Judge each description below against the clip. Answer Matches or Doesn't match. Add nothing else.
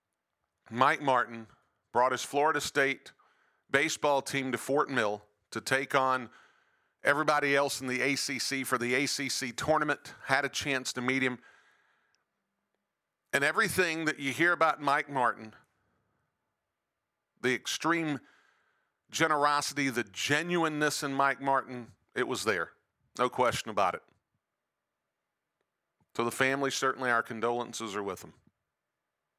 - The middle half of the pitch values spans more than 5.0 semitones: Doesn't match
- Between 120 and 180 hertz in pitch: Matches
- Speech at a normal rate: Doesn't match